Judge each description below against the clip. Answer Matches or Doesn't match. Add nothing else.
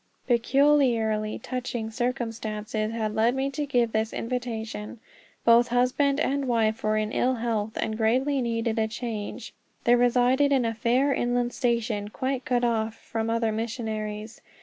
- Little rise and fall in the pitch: Matches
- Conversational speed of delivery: Matches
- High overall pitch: Matches